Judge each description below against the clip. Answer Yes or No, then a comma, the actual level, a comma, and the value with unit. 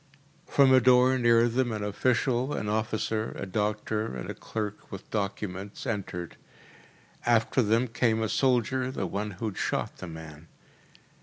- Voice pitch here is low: Yes, low, 110 Hz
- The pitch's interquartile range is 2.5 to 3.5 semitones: Yes, average, 3.1 semitones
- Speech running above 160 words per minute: No, average, 155 wpm